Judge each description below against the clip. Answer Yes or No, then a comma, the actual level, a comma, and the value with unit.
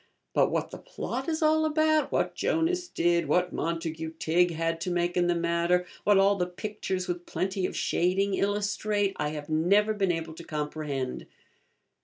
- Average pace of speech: Yes, average, 175 wpm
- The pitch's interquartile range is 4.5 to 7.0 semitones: No, average, 3.6 semitones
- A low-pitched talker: No, medium, 180 Hz